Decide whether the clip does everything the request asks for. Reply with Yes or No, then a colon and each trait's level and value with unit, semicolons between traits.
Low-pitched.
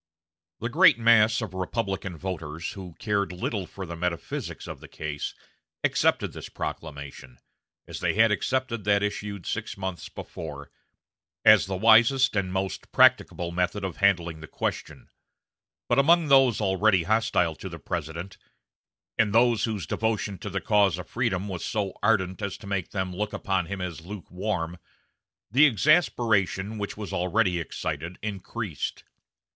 Yes: low, 100 Hz